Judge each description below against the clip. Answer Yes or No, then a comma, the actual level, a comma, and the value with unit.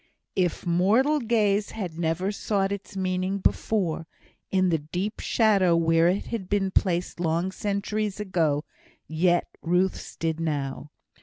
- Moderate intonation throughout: Yes, average, 3.3 semitones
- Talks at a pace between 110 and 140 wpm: Yes, slow, 135 wpm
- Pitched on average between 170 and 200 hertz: Yes, medium, 185 Hz